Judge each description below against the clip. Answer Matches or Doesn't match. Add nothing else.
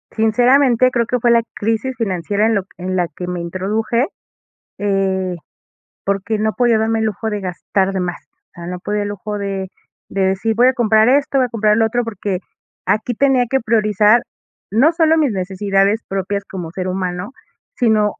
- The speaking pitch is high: Matches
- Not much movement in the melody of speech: Doesn't match